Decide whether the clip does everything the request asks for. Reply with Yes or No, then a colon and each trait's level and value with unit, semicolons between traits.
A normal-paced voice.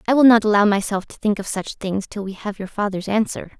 No: fast, 265 wpm